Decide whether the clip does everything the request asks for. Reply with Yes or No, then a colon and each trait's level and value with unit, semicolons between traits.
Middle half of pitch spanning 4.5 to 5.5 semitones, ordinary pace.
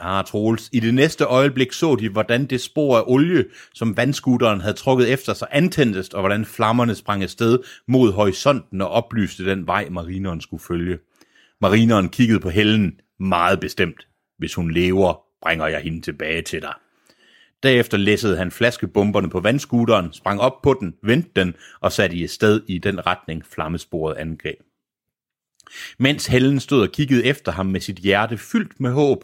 Yes: average, 5.1 semitones; average, 170 wpm